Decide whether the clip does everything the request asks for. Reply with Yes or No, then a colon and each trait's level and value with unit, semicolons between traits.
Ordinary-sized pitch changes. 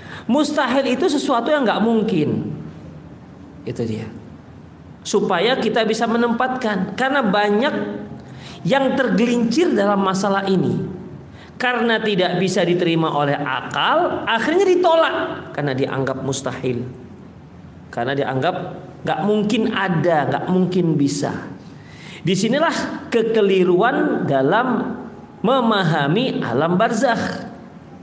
No: wide, 6.9 semitones